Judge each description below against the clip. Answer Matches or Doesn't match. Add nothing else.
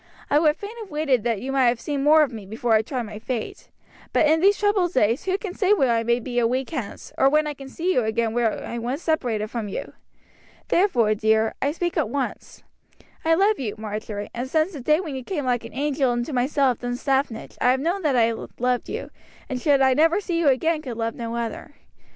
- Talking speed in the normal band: Doesn't match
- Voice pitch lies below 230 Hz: Doesn't match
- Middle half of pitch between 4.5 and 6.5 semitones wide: Matches